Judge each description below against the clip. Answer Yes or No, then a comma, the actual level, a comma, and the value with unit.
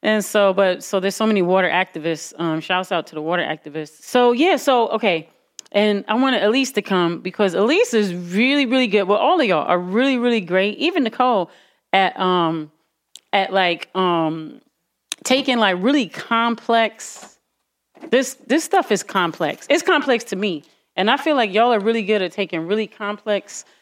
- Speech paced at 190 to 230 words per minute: No, average, 180 wpm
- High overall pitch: Yes, high, 205 Hz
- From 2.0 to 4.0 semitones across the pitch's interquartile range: No, average, 4.9 semitones